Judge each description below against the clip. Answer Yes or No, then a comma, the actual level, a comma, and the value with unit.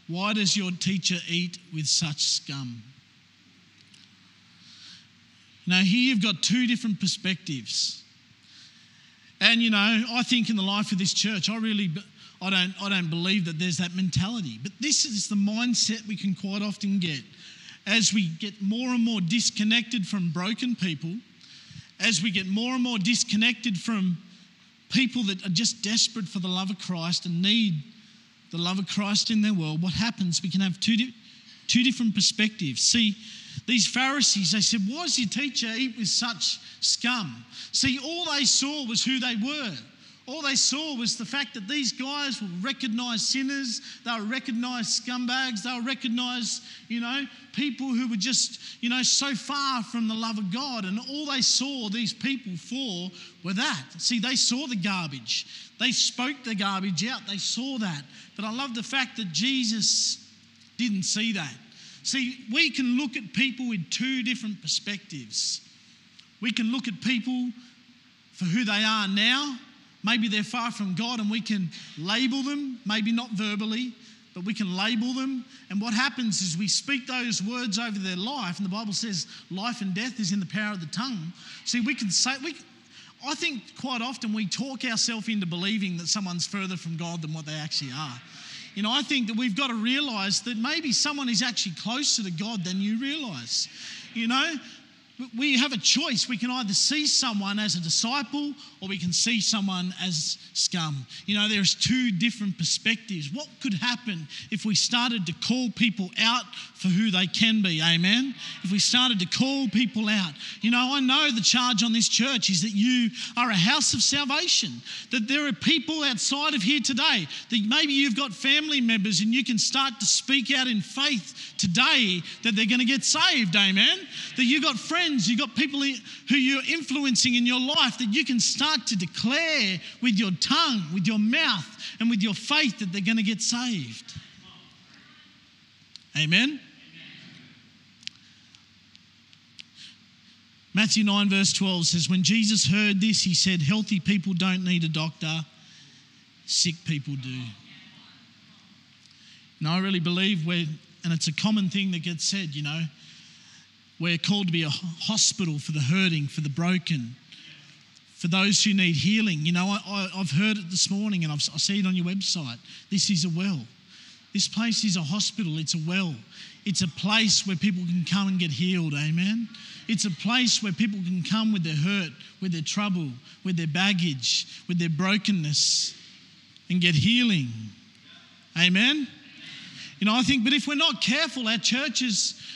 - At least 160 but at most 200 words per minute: Yes, average, 180 wpm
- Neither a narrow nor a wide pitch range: Yes, average, 4.7 semitones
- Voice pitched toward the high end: Yes, high, 215 Hz